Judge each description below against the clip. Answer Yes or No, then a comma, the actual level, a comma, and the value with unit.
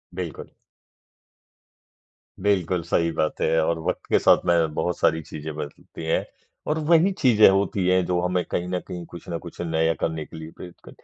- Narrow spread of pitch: Yes, narrow, 2.2 semitones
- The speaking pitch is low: Yes, very low, 85 Hz